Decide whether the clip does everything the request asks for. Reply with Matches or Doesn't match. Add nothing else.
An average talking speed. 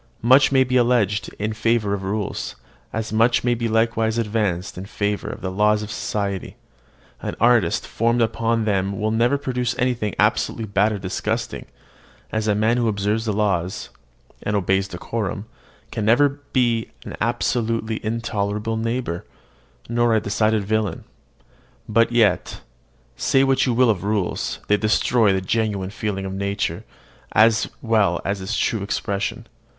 Matches